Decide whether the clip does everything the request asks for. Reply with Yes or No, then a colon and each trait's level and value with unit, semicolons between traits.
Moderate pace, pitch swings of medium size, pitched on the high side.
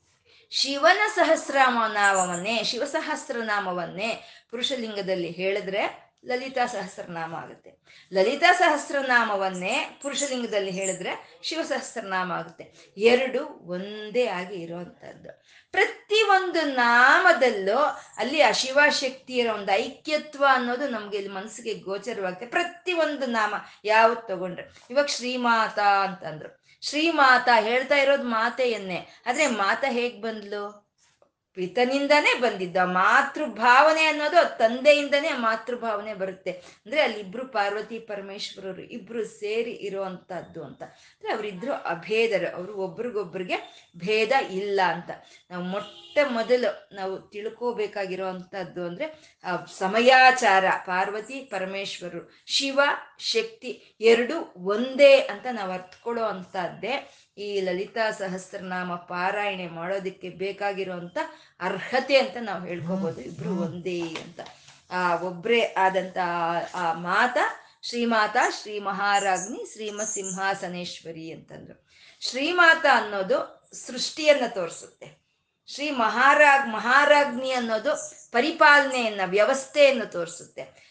No: average, 90 wpm; wide, 6.0 semitones; high, 220 Hz